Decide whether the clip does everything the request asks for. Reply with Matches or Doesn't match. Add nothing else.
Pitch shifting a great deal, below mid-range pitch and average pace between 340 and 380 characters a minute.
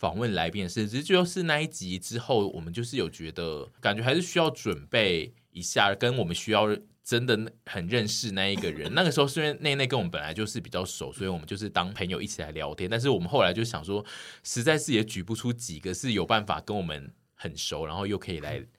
Matches